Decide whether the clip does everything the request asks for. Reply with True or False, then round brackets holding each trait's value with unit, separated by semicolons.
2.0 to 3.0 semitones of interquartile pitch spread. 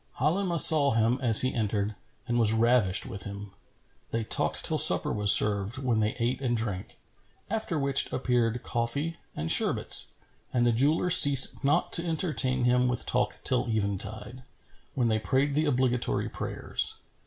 False (4.0 semitones)